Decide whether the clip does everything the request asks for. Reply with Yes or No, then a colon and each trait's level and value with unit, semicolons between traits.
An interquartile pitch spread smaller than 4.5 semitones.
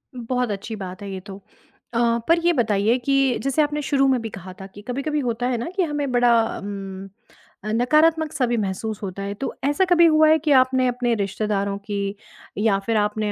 No: wide, 5.6 semitones